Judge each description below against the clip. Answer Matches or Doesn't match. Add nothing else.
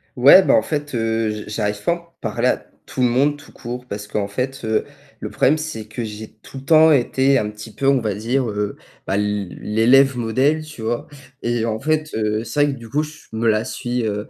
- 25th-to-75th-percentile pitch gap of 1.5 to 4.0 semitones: Doesn't match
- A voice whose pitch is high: Doesn't match